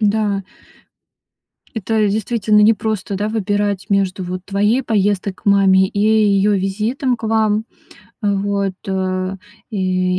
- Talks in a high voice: Yes, high, 205 Hz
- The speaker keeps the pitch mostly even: Yes, narrow, 1.8 semitones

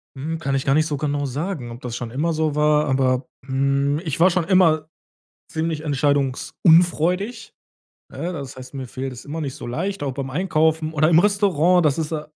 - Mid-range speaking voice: Yes, medium, 150 Hz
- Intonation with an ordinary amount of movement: Yes, average, 3.3 semitones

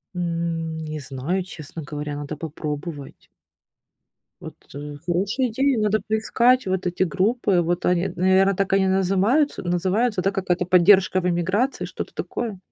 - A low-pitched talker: No, medium, 185 Hz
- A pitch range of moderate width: Yes, average, 3.3 semitones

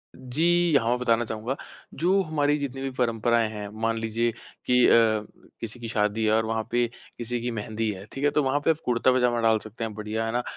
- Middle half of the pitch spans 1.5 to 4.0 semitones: Yes, average, 2.7 semitones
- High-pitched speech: No, low, 120 Hz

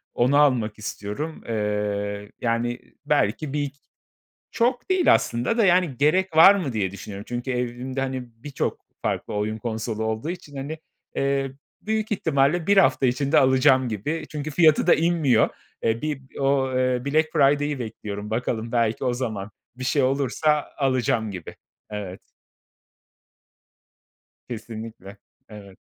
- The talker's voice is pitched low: Yes, low, 130 Hz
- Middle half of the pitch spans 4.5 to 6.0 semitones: Yes, average, 5.1 semitones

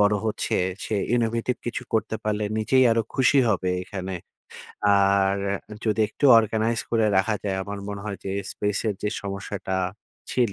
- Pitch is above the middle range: No, low, 105 Hz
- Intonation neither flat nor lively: No, narrow, 2.3 semitones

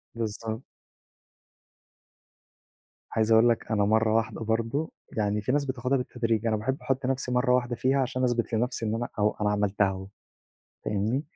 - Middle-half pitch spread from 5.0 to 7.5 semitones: No, average, 2.7 semitones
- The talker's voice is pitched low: Yes, low, 115 Hz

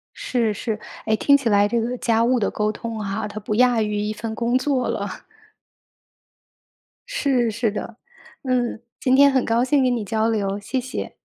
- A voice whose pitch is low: No, high, 230 Hz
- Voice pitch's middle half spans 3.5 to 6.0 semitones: No, average, 2.8 semitones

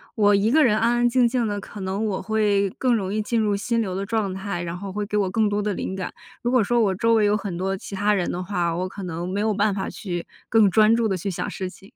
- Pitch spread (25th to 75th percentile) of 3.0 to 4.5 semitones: No, narrow, 2.4 semitones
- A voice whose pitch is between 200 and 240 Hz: Yes, high, 205 Hz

